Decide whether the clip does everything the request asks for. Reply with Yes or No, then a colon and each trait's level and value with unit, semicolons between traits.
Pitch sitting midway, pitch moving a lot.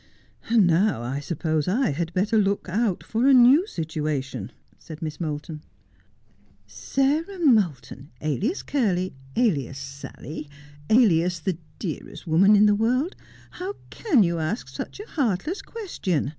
Yes: medium, 180 Hz; wide, 7.9 semitones